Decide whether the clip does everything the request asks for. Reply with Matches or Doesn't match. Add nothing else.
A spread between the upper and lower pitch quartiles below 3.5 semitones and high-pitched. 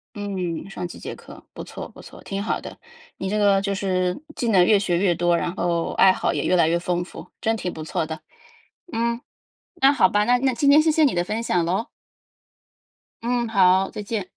Doesn't match